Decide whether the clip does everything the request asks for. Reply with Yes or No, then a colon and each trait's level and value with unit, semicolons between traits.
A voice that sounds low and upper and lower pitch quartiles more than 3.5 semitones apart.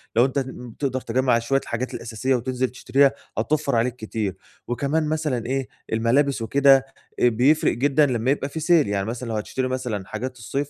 No: low, 130 Hz; average, 2.9 semitones